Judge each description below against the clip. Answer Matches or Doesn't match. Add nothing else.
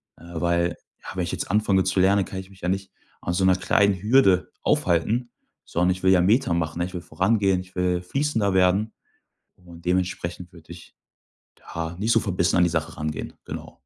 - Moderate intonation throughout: Doesn't match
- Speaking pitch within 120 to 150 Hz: Doesn't match